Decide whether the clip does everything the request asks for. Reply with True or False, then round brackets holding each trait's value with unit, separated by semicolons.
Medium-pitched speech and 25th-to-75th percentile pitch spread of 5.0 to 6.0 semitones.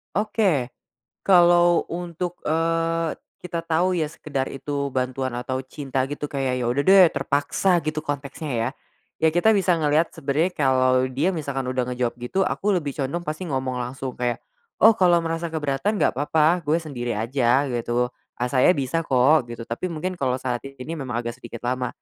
False (145 Hz; 4.6 semitones)